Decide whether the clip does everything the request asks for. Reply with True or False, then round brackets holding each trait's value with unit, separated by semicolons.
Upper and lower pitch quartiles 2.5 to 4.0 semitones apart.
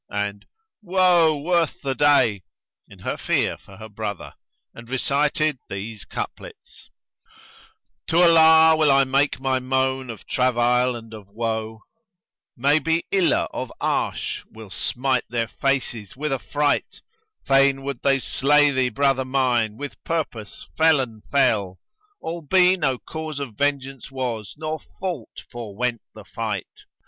False (4.6 semitones)